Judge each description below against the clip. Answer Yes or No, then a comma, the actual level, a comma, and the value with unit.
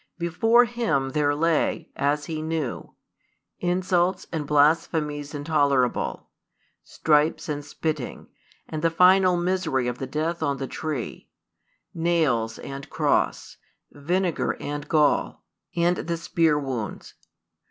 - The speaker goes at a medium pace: No, slow, 115 wpm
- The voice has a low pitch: No, medium, 155 Hz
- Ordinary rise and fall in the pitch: Yes, average, 3.1 semitones